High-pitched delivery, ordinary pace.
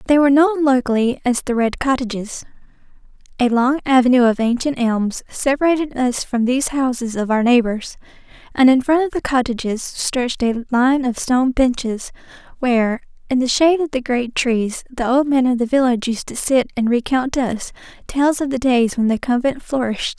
Yes: very high, 250 Hz; average, 185 wpm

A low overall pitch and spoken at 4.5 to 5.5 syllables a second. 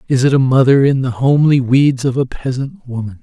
No: low, 130 Hz; 5.8 syllables/s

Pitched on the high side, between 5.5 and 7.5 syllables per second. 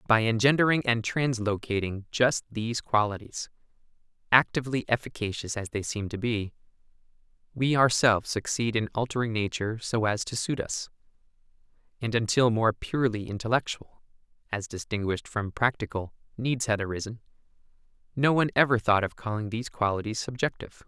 No: low, 115 Hz; 5.6 syllables/s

